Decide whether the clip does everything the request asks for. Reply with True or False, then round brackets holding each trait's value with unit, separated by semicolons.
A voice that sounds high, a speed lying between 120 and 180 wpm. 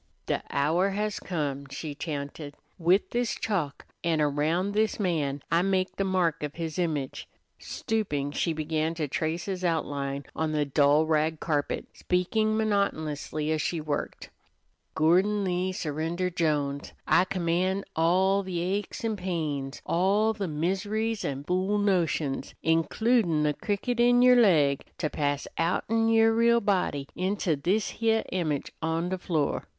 False (170 Hz; 150 wpm)